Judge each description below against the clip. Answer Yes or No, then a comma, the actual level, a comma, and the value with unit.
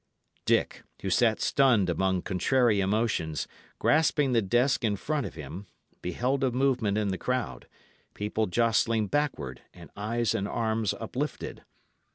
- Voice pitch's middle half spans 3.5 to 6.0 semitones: Yes, average, 4.4 semitones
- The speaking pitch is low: Yes, low, 110 Hz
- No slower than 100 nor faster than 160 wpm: Yes, average, 140 wpm